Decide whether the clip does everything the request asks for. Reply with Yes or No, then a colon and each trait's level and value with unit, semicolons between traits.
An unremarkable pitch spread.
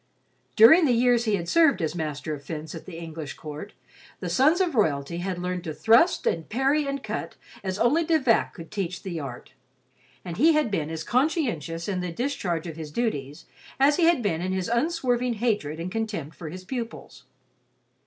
No: wide, 7.5 semitones